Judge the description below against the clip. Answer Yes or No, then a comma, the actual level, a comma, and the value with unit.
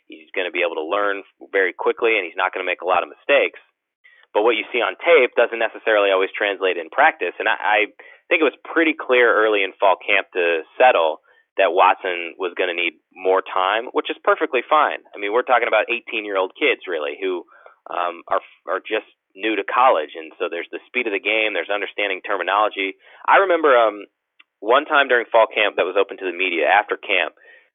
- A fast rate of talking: Yes, fast, 220 wpm